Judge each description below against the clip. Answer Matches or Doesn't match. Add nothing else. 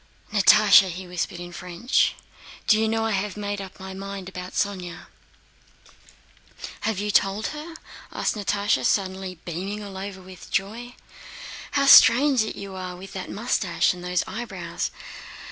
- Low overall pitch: Doesn't match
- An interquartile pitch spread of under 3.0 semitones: Matches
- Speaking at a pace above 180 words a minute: Doesn't match